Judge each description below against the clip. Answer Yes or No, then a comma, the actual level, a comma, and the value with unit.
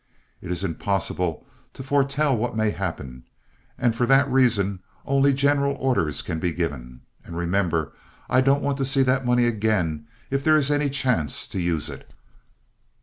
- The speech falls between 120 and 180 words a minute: Yes, average, 165 wpm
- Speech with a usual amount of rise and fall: No, wide, 7.8 semitones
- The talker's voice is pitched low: Yes, low, 115 Hz